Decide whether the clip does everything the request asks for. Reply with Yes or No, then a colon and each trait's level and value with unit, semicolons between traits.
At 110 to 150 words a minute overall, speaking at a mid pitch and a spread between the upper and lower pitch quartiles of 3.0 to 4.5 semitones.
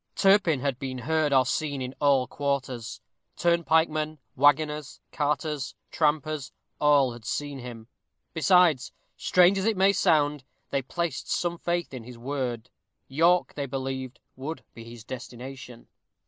Yes: average, 140 wpm; medium, 145 Hz; average, 3.7 semitones